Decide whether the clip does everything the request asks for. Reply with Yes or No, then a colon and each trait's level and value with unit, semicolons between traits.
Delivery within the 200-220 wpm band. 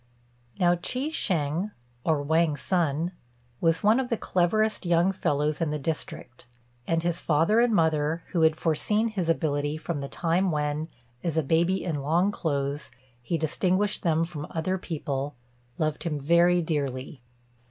No: average, 155 wpm